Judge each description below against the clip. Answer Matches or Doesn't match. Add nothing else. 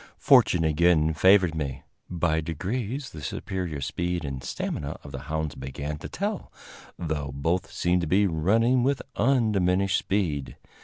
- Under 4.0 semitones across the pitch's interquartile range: Doesn't match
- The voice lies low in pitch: Matches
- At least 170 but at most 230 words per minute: Doesn't match